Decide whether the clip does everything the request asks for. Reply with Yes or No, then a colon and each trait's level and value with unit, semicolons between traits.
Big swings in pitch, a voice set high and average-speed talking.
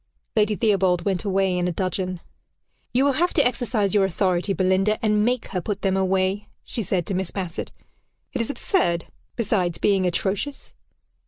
No: average, 2.7 semitones; high, 195 Hz; average, 170 wpm